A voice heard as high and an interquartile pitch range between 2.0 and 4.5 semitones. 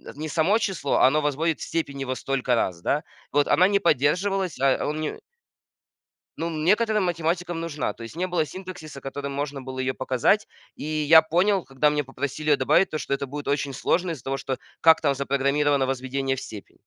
No: medium, 150 Hz; average, 3.6 semitones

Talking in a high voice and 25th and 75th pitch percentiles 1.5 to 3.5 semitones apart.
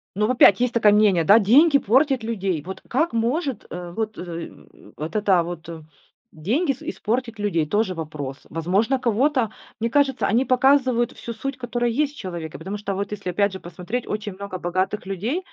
No: high, 215 Hz; average, 5.2 semitones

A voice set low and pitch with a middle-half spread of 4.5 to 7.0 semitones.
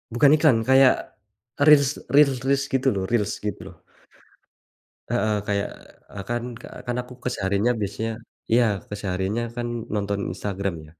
Yes: low, 115 Hz; average, 4.8 semitones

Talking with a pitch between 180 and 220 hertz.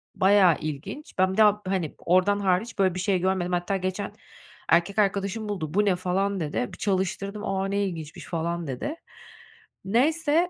Yes: high, 190 Hz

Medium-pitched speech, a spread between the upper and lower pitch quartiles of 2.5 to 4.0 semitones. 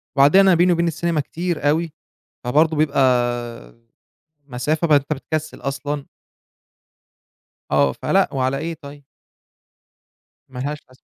Yes: medium, 145 Hz; average, 3.6 semitones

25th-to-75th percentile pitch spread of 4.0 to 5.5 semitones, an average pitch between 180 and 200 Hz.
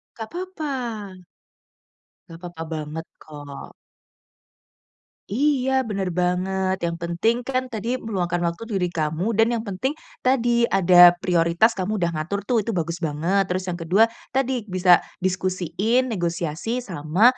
Yes: average, 5.1 semitones; high, 190 Hz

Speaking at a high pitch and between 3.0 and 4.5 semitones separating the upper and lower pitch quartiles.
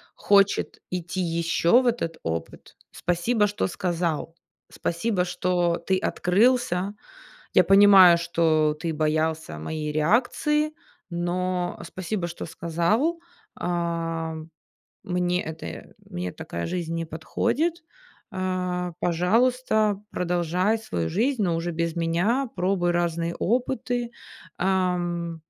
No: medium, 175 Hz; average, 3.3 semitones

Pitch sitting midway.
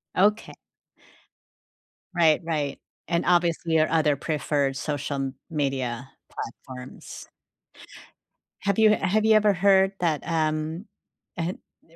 Yes: medium, 160 Hz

